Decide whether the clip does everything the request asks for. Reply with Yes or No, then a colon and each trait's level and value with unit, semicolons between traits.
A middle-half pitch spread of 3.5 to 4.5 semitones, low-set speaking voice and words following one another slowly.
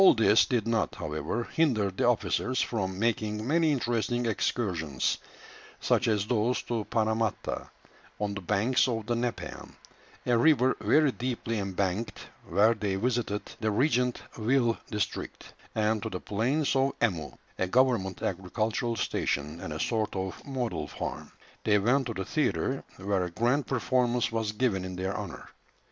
No: average, 3.8 semitones; low, 110 Hz; average, 155 wpm